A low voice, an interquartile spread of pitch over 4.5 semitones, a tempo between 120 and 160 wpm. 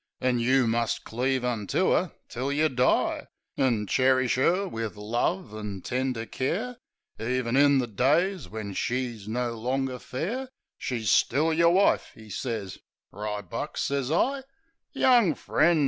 Yes: low, 130 Hz; average, 5.0 semitones; average, 140 wpm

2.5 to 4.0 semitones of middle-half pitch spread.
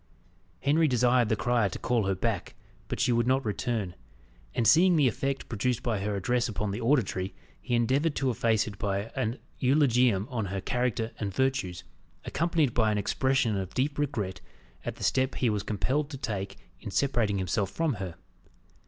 No: average, 4.4 semitones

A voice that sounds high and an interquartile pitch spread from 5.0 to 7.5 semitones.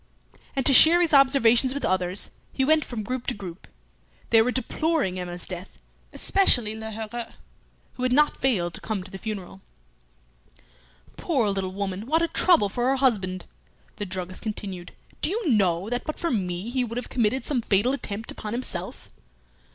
Yes: high, 225 Hz; wide, 5.6 semitones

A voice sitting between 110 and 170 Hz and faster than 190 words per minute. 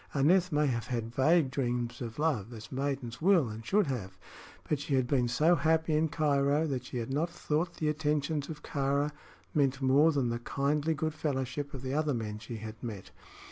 Yes: medium, 140 Hz; average, 200 wpm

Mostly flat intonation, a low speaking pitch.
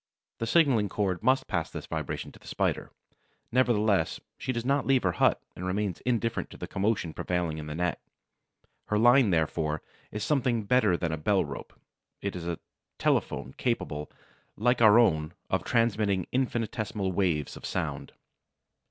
No: average, 5.3 semitones; low, 105 Hz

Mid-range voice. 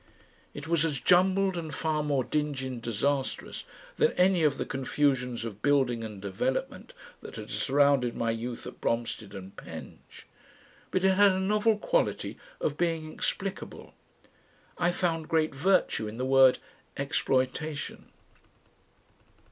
Yes: medium, 145 Hz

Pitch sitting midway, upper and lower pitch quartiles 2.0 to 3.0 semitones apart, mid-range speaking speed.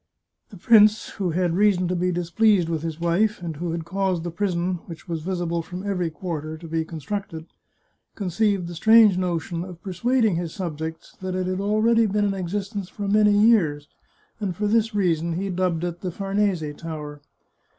No: medium, 180 Hz; average, 3.4 semitones; average, 185 wpm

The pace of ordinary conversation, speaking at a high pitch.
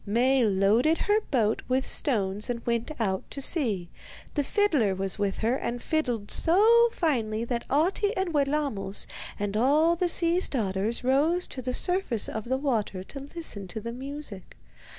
Yes: average, 165 wpm; very high, 250 Hz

